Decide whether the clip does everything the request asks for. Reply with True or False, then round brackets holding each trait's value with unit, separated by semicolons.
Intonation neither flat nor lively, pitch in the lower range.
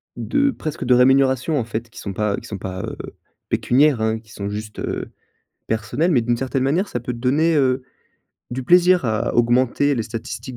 True (4.0 semitones; 125 Hz)